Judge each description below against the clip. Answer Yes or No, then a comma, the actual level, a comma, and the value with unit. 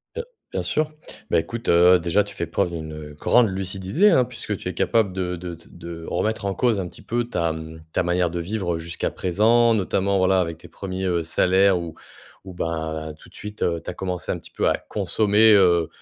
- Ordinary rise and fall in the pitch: Yes, average, 3.4 semitones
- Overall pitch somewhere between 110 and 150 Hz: No, very low, 90 Hz